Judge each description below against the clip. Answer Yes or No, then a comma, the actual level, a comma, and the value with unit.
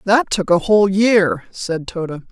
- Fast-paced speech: No, average, 180 wpm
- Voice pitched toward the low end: No, high, 190 Hz